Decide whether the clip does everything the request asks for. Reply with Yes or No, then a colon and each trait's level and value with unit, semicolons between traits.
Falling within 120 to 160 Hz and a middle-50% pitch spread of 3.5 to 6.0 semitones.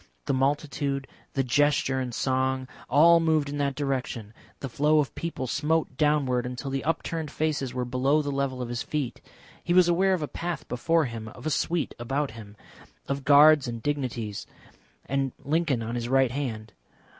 No: medium, 140 Hz; average, 3.0 semitones